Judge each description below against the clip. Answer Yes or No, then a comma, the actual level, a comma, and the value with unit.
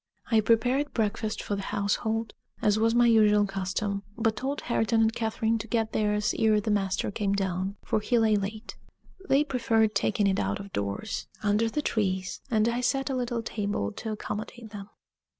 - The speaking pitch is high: Yes, high, 215 Hz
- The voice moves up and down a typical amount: No, narrow, 2.1 semitones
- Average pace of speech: Yes, average, 185 wpm